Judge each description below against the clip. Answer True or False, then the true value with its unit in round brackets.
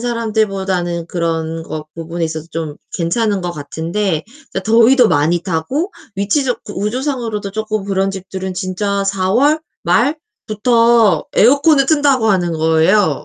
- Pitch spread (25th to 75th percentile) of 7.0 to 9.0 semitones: False (5.5 semitones)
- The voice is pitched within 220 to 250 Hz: False (195 Hz)